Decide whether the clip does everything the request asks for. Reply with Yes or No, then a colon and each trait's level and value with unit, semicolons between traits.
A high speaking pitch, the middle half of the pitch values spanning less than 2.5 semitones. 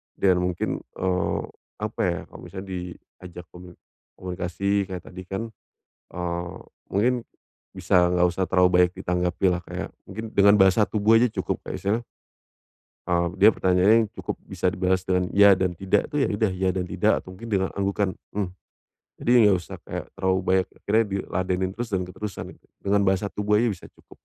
No: very low, 95 Hz; narrow, 2.0 semitones